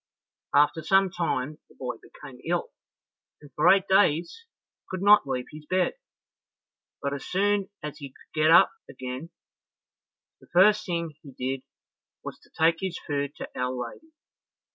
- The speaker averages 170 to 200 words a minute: No, average, 155 wpm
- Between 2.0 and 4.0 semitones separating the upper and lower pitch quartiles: No, average, 5.3 semitones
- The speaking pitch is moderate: Yes, medium, 155 Hz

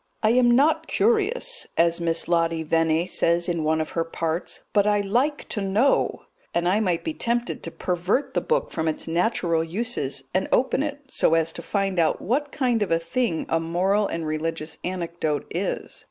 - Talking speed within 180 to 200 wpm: Yes, average, 190 wpm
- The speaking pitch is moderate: Yes, medium, 180 Hz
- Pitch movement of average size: No, wide, 6.4 semitones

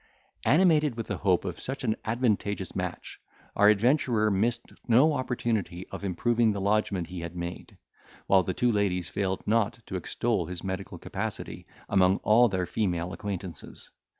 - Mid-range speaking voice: No, low, 105 Hz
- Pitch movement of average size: Yes, average, 4.2 semitones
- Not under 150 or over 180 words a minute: Yes, average, 155 wpm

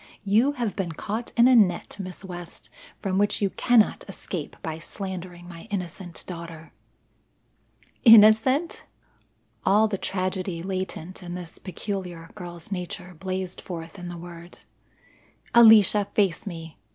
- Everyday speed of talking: No, slow, 130 wpm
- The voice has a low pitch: No, medium, 185 Hz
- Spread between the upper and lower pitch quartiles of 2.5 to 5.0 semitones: Yes, average, 2.9 semitones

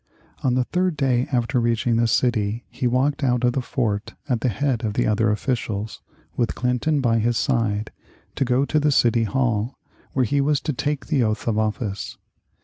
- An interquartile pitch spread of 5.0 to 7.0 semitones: No, average, 3.1 semitones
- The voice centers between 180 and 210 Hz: No, low, 120 Hz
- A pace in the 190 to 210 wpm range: Yes, average, 195 wpm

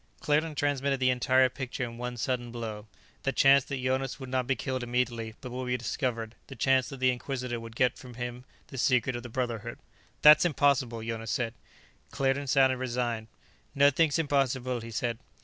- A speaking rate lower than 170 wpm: No, average, 185 wpm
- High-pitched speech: No, low, 125 Hz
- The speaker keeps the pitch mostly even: Yes, narrow, 2.1 semitones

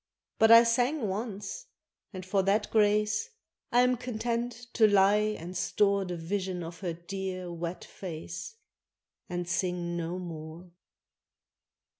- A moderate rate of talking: No, slow, 130 wpm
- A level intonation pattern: No, average, 3.7 semitones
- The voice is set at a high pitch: Yes, high, 195 Hz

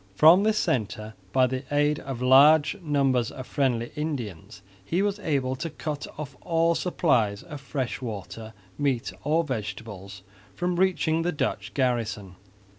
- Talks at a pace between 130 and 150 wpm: Yes, average, 145 wpm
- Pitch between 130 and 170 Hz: Yes, low, 135 Hz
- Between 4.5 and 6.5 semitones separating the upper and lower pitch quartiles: Yes, wide, 5.6 semitones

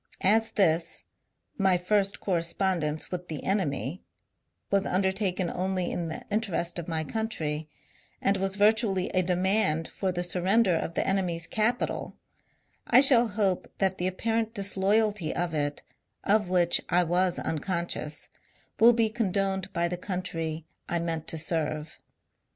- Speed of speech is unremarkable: Yes, average, 145 wpm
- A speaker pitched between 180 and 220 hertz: Yes, medium, 185 Hz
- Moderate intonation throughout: Yes, average, 3.1 semitones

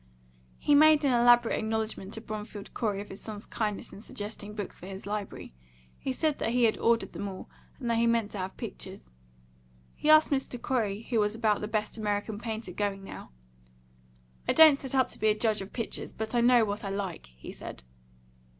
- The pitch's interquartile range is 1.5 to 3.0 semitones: Yes, average, 2.7 semitones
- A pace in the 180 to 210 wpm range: Yes, fast, 205 wpm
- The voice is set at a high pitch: Yes, high, 220 Hz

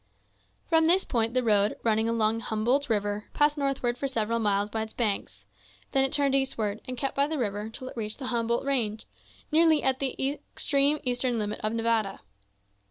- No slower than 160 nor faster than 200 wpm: Yes, average, 185 wpm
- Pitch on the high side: Yes, high, 235 Hz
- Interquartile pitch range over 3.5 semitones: Yes, average, 4.0 semitones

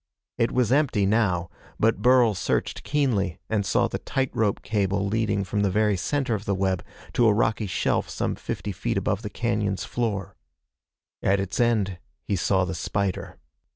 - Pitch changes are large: No, average, 3.1 semitones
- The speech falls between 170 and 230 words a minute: Yes, average, 175 wpm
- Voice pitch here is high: No, low, 105 Hz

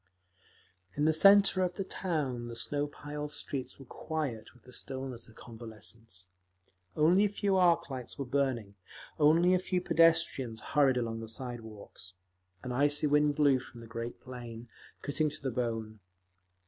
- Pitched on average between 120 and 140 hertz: Yes, low, 135 Hz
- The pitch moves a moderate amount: Yes, average, 4.8 semitones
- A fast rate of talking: No, average, 160 wpm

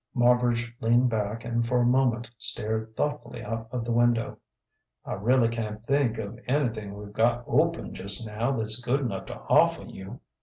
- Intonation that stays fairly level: Yes, narrow, 1.9 semitones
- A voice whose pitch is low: Yes, low, 115 Hz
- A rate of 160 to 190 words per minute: Yes, average, 175 wpm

